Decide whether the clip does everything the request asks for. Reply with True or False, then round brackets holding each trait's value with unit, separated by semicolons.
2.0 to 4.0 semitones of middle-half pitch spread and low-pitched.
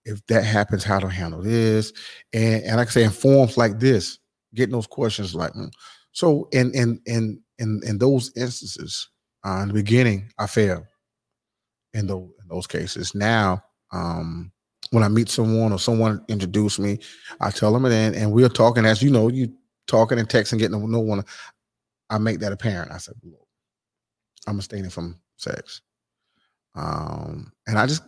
True (2.4 semitones; 110 Hz)